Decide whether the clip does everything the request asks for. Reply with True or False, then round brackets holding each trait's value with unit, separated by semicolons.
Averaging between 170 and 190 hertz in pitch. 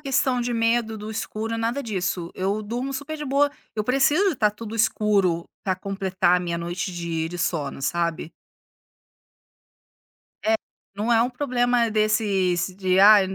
False (215 Hz)